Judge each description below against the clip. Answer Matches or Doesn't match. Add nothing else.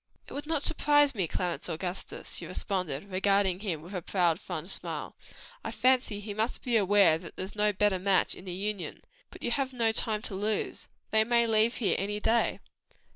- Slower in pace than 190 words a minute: Doesn't match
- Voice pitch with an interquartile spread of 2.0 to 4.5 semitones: Matches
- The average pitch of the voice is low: Doesn't match